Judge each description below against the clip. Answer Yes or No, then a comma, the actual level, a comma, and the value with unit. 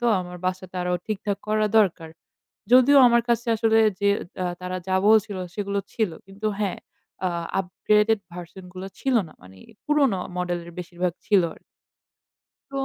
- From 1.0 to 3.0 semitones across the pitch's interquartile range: No, average, 3.4 semitones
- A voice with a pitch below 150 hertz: No, high, 200 Hz